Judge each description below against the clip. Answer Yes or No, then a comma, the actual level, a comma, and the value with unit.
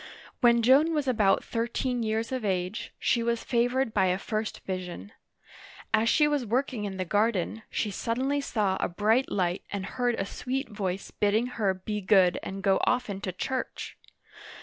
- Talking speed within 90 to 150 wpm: No, average, 175 wpm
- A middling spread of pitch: Yes, average, 4.2 semitones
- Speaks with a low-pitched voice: No, high, 220 Hz